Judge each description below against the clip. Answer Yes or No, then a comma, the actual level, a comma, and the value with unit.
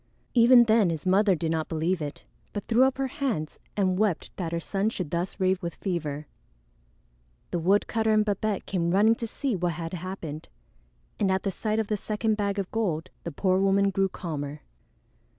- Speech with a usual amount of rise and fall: Yes, average, 4.0 semitones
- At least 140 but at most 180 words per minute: No, average, 190 wpm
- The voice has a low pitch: No, high, 190 Hz